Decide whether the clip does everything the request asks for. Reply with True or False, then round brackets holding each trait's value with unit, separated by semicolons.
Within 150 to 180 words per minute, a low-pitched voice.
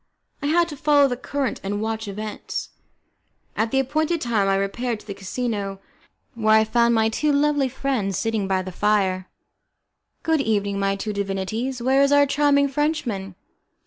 False (170 wpm; 225 Hz)